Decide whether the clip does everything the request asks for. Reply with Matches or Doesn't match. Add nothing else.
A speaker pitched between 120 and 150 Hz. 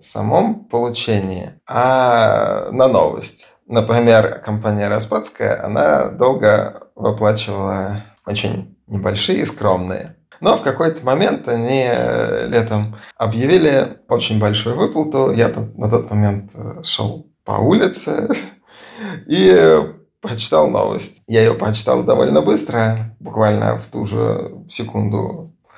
Doesn't match